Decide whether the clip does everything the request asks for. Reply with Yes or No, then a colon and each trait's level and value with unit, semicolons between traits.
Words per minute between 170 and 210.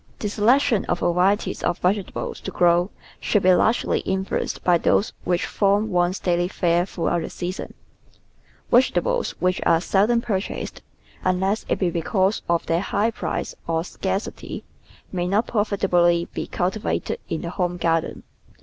No: average, 155 wpm